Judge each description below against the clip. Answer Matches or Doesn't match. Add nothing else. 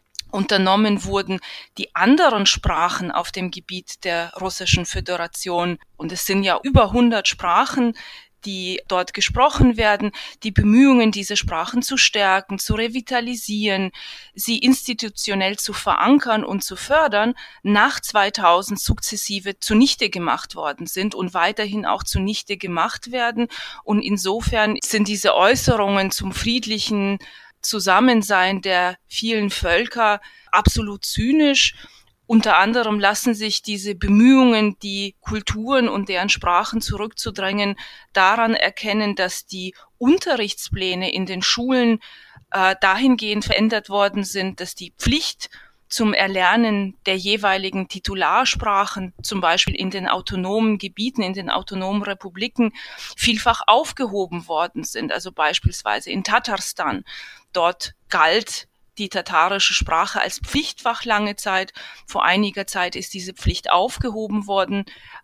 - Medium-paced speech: Doesn't match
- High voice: Matches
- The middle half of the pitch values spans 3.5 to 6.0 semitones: Doesn't match